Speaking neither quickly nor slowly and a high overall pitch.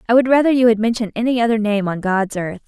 No: fast, 270 wpm; high, 225 Hz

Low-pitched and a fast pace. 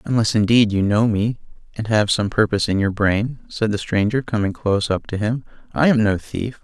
Yes: low, 110 Hz; fast, 215 wpm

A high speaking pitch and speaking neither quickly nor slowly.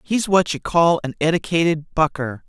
No: medium, 160 Hz; average, 170 wpm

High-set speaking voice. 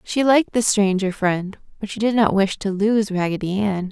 Yes: high, 205 Hz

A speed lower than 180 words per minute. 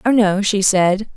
No: fast, 205 wpm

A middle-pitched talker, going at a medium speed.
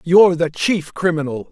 Yes: medium, 165 Hz; average, 160 wpm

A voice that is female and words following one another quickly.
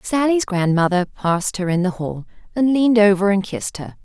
No: female; average, 195 wpm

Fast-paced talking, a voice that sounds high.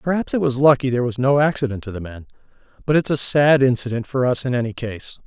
No: fast, 240 wpm; low, 130 Hz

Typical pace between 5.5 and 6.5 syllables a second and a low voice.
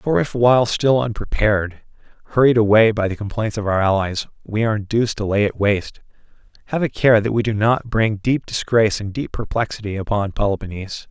Yes: 5.9 syllables/s; low, 110 Hz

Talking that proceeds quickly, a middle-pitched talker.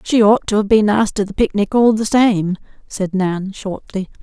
No: fast, 215 wpm; high, 205 Hz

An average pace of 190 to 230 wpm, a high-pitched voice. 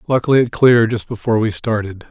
No: average, 200 wpm; low, 115 Hz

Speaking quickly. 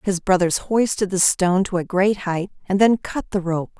Yes: fast, 220 wpm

